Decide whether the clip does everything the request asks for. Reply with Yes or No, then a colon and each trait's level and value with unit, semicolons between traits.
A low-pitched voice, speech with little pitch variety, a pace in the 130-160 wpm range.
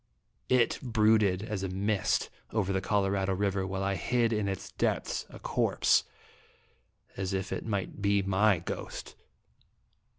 Yes: low, 100 Hz; narrow, 2.0 semitones; average, 140 wpm